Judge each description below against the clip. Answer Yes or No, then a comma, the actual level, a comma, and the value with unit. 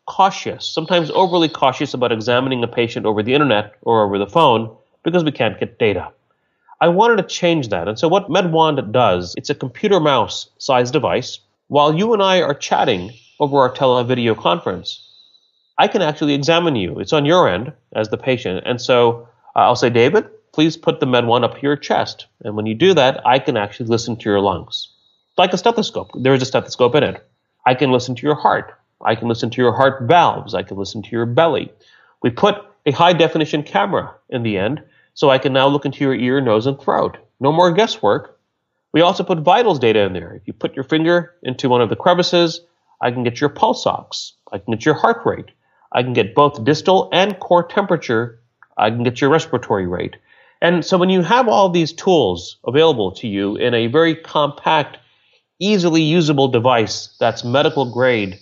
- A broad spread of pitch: Yes, wide, 6.1 semitones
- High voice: No, medium, 140 Hz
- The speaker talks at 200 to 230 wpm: Yes, fast, 205 wpm